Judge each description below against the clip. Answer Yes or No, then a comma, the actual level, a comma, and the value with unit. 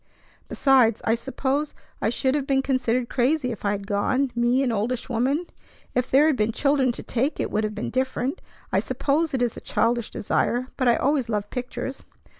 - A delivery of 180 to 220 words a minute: Yes, average, 200 wpm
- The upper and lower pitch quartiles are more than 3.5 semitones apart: No, average, 2.9 semitones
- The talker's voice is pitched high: Yes, very high, 255 Hz